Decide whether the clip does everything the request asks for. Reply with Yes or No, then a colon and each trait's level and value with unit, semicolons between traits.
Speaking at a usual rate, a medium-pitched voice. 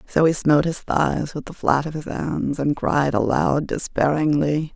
Yes: average, 190 wpm; medium, 145 Hz